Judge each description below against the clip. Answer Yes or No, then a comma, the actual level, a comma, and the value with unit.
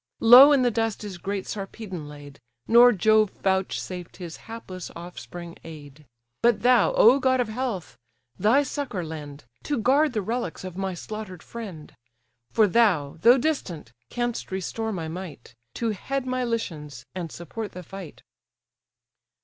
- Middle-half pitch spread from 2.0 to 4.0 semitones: No, wide, 5.5 semitones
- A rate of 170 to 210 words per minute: No, average, 150 wpm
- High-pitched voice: Yes, high, 200 Hz